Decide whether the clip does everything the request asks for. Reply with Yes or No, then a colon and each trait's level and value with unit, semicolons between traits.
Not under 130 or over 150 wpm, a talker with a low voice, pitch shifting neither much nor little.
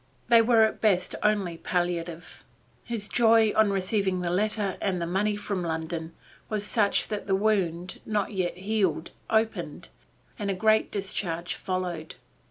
No: average, 145 wpm; high, 195 Hz; average, 3.3 semitones